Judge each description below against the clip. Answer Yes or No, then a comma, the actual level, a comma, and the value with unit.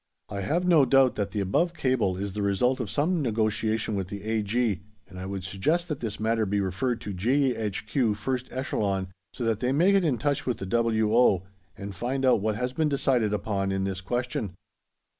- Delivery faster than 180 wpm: Yes, average, 200 wpm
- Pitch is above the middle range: No, low, 110 Hz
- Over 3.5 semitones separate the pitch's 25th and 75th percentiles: Yes, average, 4.6 semitones